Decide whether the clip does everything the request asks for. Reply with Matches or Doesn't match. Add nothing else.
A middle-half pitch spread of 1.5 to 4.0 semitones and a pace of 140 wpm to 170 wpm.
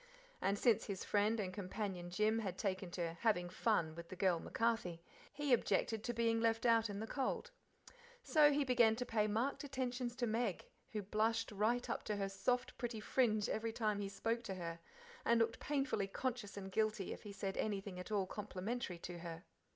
Doesn't match